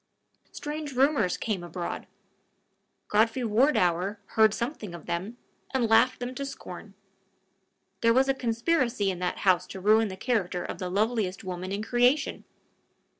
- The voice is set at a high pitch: Yes, high, 220 Hz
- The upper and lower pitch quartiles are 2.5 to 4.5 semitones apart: No, average, 5.0 semitones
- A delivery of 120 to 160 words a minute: Yes, average, 145 wpm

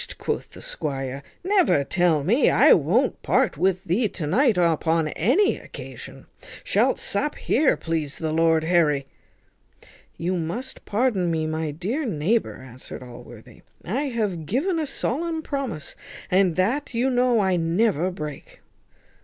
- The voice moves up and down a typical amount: No, wide, 7.8 semitones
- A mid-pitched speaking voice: Yes, medium, 180 Hz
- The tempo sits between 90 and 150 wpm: Yes, average, 140 wpm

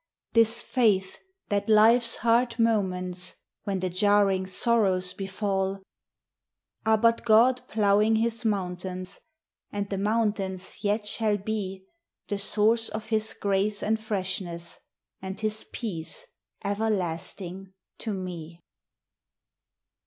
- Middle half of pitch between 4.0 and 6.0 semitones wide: No, average, 2.7 semitones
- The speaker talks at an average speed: No, slow, 110 wpm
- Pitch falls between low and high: No, high, 205 Hz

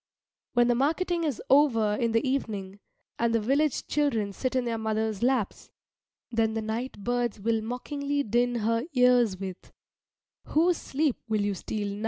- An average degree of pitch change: Yes, average, 3.5 semitones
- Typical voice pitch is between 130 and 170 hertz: No, high, 235 Hz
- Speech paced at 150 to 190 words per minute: Yes, average, 165 wpm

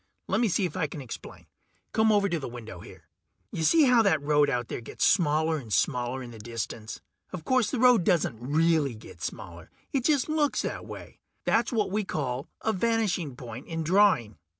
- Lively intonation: Yes, wide, 9.0 semitones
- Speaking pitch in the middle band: Yes, medium, 160 Hz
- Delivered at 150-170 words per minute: No, average, 195 wpm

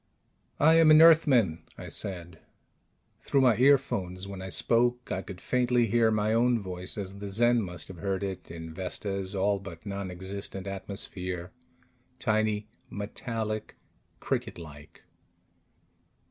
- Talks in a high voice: No, low, 100 Hz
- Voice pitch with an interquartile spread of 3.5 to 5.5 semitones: Yes, average, 4.0 semitones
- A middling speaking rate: No, slow, 130 wpm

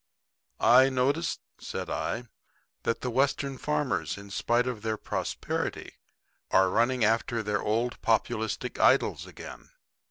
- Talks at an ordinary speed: No, slow, 125 wpm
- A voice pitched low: Yes, low, 120 Hz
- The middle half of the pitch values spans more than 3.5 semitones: No, average, 3.0 semitones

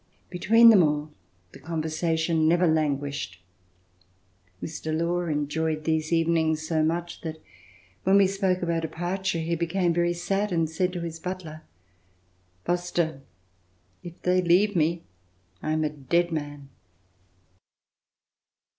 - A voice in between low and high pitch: Yes, medium, 165 Hz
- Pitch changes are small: Yes, narrow, 2.0 semitones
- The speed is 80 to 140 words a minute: Yes, slow, 135 wpm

